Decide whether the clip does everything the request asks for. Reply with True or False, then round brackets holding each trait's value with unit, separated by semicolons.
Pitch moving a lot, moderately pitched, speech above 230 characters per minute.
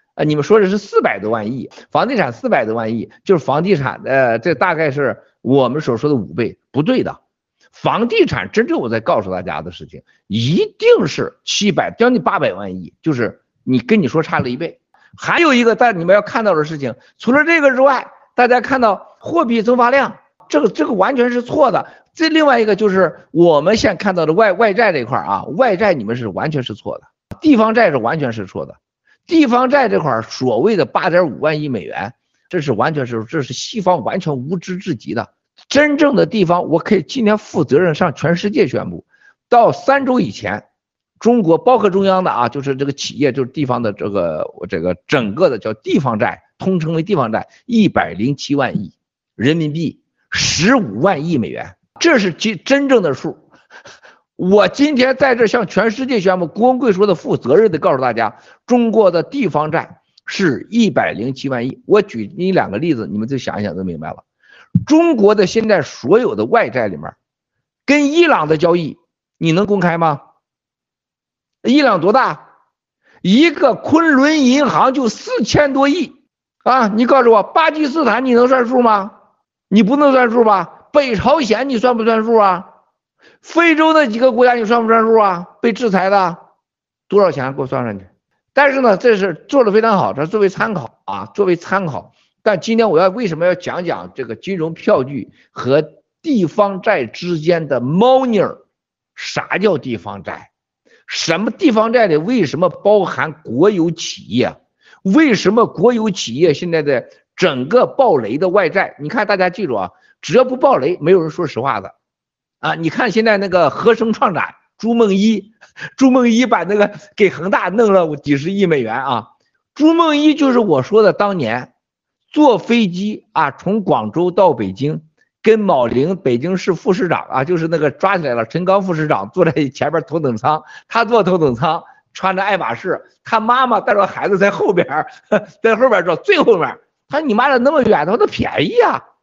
False (6.8 semitones; 205 Hz; 275 characters per minute)